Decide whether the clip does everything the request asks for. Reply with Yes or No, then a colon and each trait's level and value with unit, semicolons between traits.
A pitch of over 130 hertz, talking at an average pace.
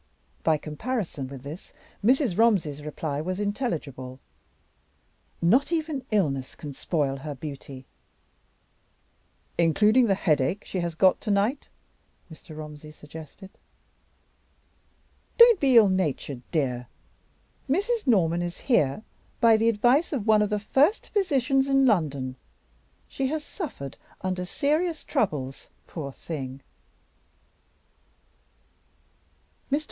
No: medium, 185 Hz; slow, 110 wpm